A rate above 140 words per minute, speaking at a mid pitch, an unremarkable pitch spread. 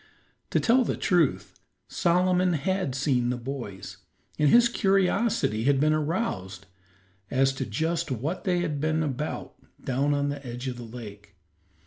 No: average, 150 wpm; medium, 145 Hz; wide, 6.2 semitones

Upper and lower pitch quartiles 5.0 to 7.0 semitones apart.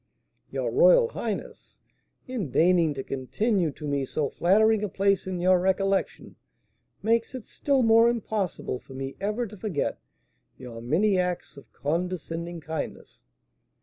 Yes: wide, 5.6 semitones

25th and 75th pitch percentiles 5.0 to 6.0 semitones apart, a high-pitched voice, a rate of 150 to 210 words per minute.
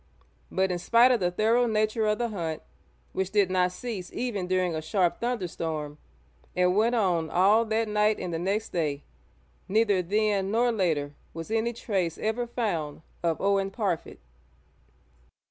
No: average, 3.9 semitones; high, 195 Hz; average, 160 wpm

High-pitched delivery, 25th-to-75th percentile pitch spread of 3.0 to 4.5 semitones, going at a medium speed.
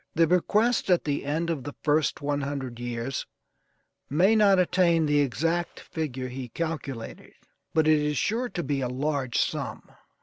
No: medium, 150 Hz; average, 3.9 semitones; average, 165 wpm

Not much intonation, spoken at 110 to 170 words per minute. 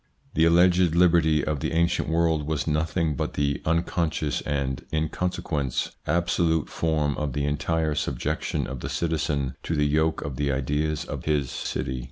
Yes: narrow, 2.2 semitones; average, 165 wpm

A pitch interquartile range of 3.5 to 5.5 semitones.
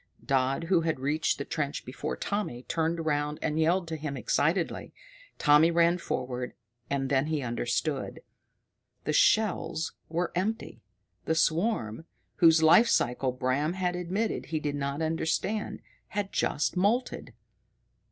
Yes: average, 4.0 semitones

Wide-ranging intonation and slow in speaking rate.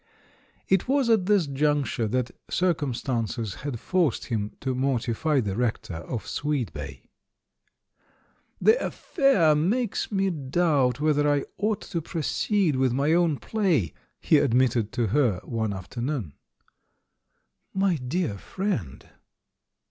Yes: wide, 6.7 semitones; slow, 120 wpm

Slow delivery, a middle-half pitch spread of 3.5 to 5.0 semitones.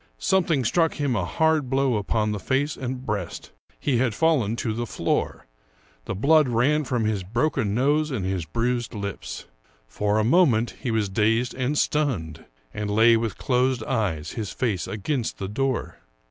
No: average, 170 wpm; average, 4.4 semitones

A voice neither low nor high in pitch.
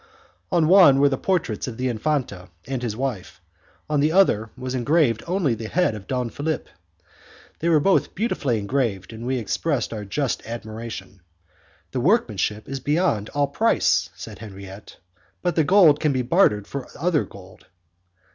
No: low, 130 Hz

